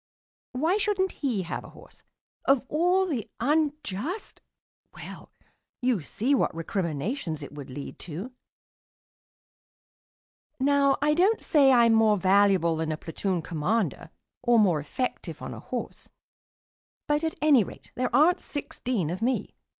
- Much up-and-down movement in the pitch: Yes, wide, 8.5 semitones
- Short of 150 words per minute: Yes, slow, 135 wpm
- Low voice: No, high, 240 Hz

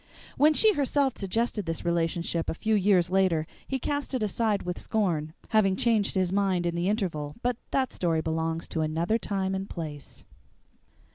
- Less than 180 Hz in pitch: No, high, 190 Hz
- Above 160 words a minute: Yes, average, 170 wpm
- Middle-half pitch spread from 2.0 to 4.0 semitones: No, average, 4.8 semitones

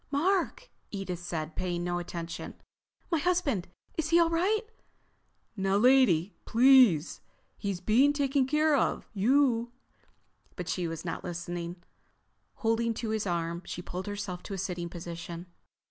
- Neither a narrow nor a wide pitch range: No, wide, 7.5 semitones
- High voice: Yes, high, 200 Hz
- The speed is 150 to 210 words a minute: No, average, 140 wpm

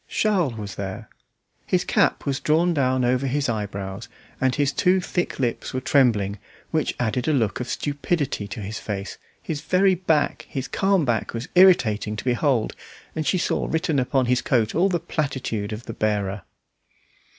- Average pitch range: No, wide, 6.3 semitones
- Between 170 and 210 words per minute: Yes, average, 175 wpm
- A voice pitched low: Yes, low, 130 Hz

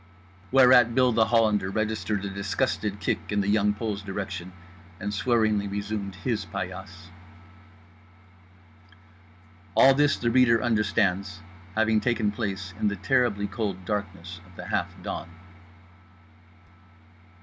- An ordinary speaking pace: No, slow, 125 wpm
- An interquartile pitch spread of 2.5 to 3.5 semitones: Yes, average, 2.8 semitones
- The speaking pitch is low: Yes, low, 105 Hz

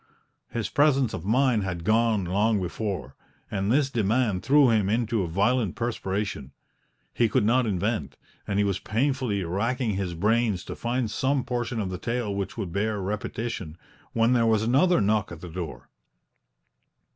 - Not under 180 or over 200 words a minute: No, average, 165 wpm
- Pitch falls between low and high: No, low, 110 Hz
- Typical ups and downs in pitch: Yes, average, 3.7 semitones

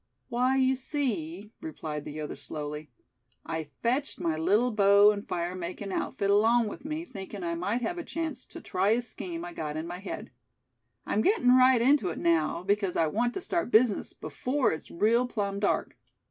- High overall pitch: Yes, high, 205 Hz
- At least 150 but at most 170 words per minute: No, average, 190 wpm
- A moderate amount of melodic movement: No, wide, 6.6 semitones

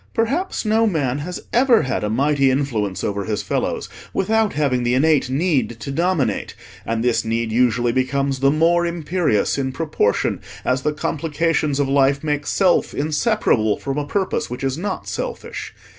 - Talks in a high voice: No, medium, 140 Hz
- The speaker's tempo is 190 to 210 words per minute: No, average, 165 wpm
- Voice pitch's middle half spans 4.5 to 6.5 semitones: Yes, average, 5.0 semitones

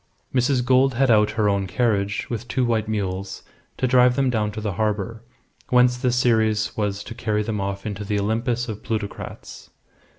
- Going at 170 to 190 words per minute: Yes, average, 185 wpm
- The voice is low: Yes, low, 110 Hz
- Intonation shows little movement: No, average, 3.1 semitones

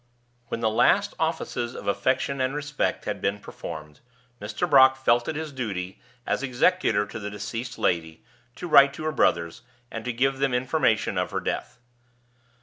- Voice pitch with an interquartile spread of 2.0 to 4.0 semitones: No, average, 5.1 semitones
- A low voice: Yes, low, 125 Hz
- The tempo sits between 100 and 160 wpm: No, average, 170 wpm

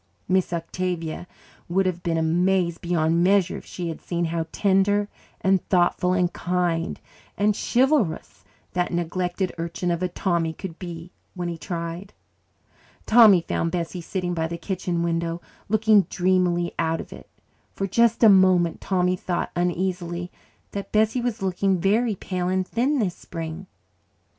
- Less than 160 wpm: Yes, average, 150 wpm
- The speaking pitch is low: No, medium, 180 Hz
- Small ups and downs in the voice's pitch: Yes, narrow, 2.1 semitones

